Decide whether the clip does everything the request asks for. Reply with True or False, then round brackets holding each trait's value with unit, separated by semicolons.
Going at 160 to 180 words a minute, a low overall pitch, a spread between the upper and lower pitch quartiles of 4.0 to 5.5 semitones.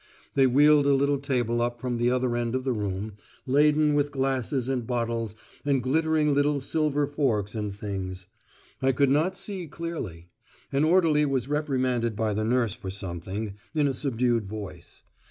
True (170 wpm; 130 Hz; 4.5 semitones)